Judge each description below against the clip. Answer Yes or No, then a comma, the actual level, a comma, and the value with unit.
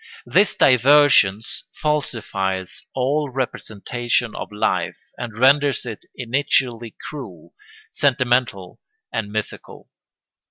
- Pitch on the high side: No, low, 125 Hz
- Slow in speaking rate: Yes, slow, 90 wpm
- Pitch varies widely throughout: No, average, 4.2 semitones